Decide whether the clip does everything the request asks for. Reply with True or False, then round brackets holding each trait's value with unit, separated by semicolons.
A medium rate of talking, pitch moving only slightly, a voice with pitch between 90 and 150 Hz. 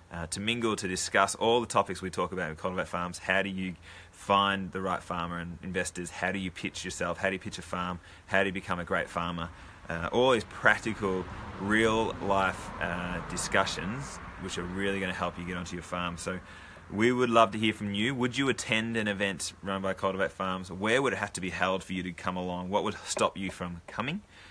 False (230 wpm; 2.2 semitones; 95 Hz)